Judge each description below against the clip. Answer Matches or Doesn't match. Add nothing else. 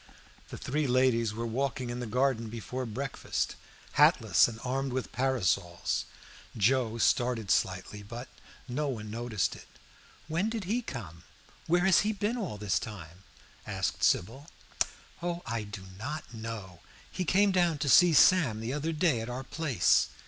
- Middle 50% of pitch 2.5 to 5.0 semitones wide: Doesn't match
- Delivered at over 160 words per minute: Doesn't match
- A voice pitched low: Matches